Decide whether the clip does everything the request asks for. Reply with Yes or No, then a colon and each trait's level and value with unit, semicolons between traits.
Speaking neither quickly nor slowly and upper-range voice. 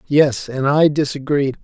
No: average, 145 wpm; medium, 140 Hz